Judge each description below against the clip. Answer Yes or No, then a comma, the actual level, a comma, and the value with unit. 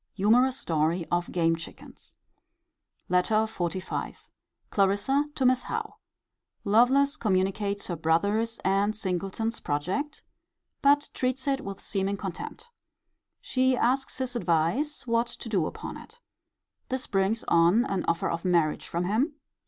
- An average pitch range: No, wide, 6.0 semitones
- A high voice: Yes, high, 205 Hz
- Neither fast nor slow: No, slow, 130 wpm